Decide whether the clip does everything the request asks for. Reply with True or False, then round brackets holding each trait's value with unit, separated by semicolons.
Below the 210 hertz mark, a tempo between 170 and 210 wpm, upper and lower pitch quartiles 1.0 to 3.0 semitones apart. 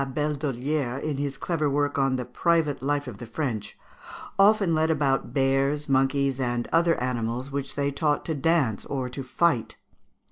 True (140 Hz; 175 wpm; 2.5 semitones)